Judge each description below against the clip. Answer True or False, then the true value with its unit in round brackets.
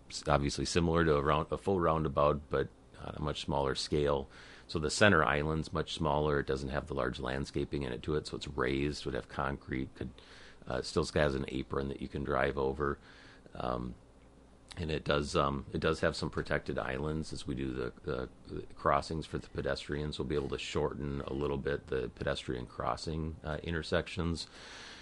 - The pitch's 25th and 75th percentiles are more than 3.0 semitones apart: False (2.6 semitones)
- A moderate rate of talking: True (195 wpm)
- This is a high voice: False (75 Hz)